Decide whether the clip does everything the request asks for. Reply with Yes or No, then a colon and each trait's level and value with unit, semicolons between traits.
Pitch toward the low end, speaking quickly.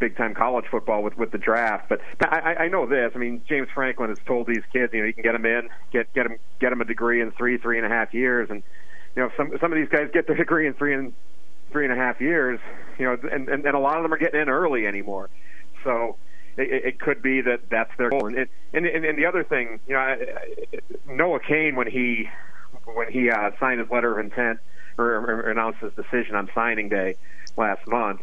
Yes: low, 125 Hz; fast, 240 wpm